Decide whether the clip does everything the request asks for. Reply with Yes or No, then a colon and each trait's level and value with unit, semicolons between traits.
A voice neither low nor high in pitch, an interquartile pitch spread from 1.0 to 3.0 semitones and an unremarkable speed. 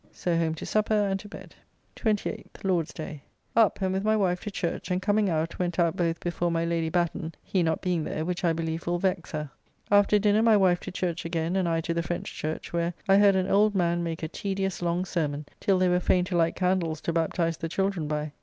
No: medium, 175 Hz; average, 2.7 semitones; fast, 240 wpm